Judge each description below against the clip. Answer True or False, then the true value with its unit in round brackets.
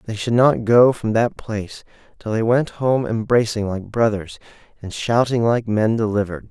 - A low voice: True (110 Hz)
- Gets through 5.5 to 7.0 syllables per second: False (4.8 syllables/s)